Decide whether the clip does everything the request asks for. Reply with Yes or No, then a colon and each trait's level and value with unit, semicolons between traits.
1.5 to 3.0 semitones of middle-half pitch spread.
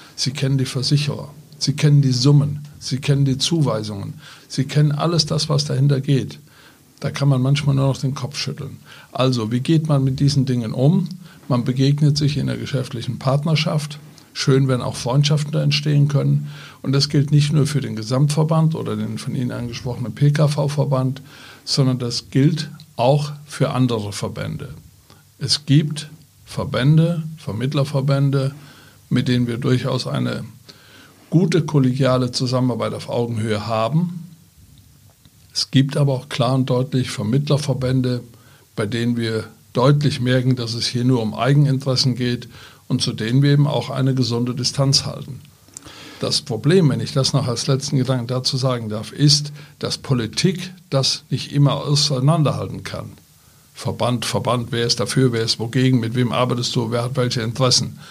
Yes: average, 2.7 semitones